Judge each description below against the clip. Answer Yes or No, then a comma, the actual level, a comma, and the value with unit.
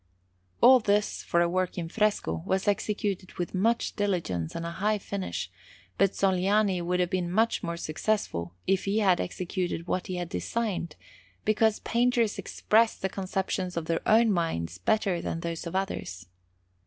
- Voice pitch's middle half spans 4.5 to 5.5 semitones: No, average, 3.6 semitones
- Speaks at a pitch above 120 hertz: Yes, medium, 185 Hz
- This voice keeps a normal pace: Yes, average, 165 wpm